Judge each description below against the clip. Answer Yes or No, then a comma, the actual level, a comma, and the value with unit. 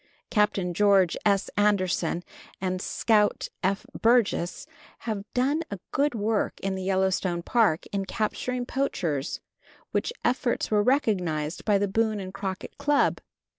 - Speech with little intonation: No, average, 3.4 semitones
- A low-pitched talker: No, high, 200 Hz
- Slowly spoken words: Yes, slow, 130 wpm